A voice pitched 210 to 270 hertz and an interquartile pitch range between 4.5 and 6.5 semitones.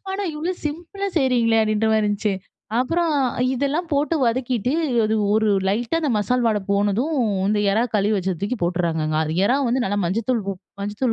Yes: high, 230 Hz; average, 4.8 semitones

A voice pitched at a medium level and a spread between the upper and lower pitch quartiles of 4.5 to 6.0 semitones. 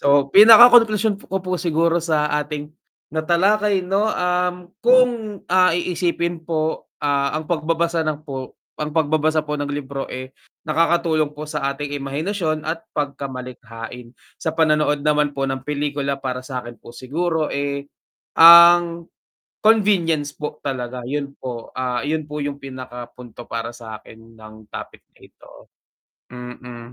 No: medium, 150 Hz; average, 3.9 semitones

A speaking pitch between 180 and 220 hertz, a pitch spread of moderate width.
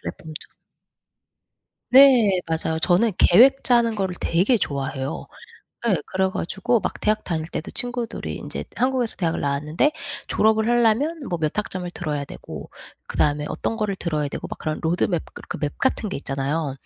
No: medium, 185 Hz; wide, 6.7 semitones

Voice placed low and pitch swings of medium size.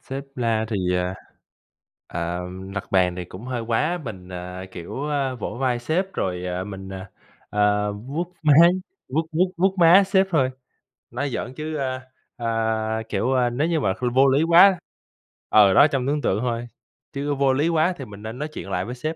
No: low, 125 Hz; wide, 6.6 semitones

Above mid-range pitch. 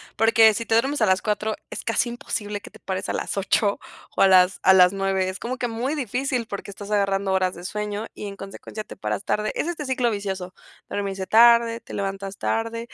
Yes: high, 205 Hz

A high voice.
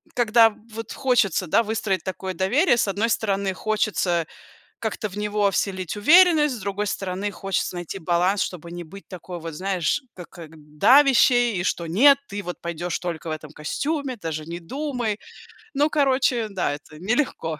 Yes: high, 195 Hz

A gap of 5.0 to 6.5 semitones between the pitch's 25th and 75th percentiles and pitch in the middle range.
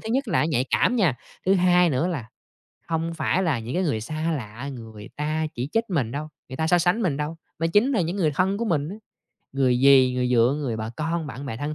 Yes: wide, 5.5 semitones; medium, 155 Hz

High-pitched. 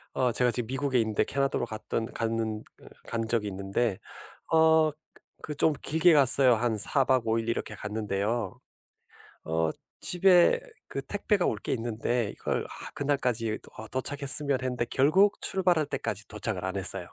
No: low, 120 Hz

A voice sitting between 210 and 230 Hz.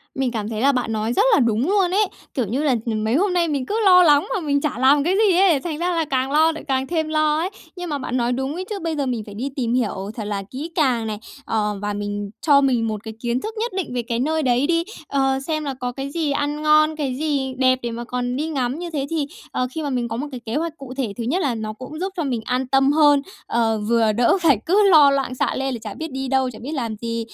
No: very high, 270 Hz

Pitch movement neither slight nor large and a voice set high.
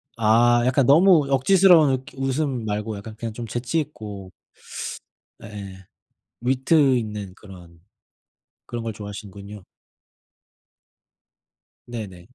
No: average, 4.5 semitones; low, 115 Hz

